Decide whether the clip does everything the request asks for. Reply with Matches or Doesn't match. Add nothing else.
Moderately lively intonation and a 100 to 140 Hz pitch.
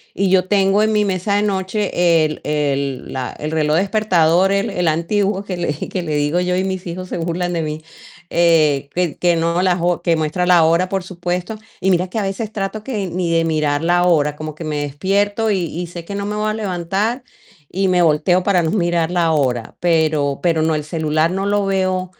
Doesn't match